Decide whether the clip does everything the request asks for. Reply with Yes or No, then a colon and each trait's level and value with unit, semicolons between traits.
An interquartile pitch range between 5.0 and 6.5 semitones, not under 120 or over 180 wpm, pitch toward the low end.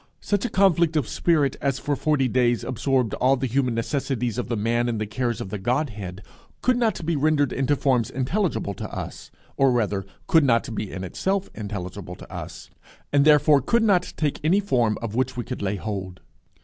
No: wide, 5.4 semitones; average, 200 wpm; low, 130 Hz